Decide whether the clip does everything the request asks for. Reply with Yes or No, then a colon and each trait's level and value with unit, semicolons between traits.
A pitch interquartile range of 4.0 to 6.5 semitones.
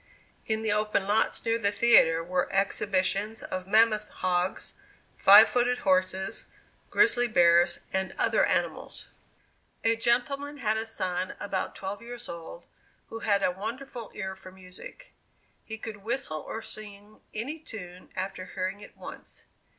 No: average, 3.4 semitones